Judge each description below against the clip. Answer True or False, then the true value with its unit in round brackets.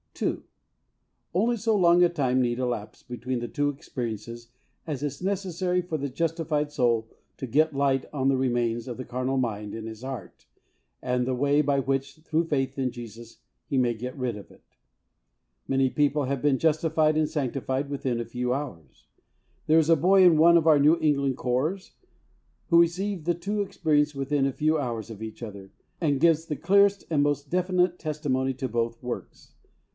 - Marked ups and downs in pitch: False (4.5 semitones)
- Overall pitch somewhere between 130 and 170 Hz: True (140 Hz)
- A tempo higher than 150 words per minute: True (185 wpm)